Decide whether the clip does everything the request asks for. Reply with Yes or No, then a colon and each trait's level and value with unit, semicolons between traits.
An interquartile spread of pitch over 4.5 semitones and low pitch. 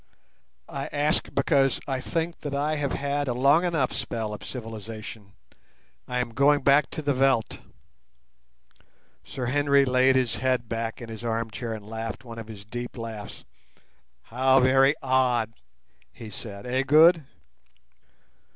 No: average, 3.7 semitones; low, 130 Hz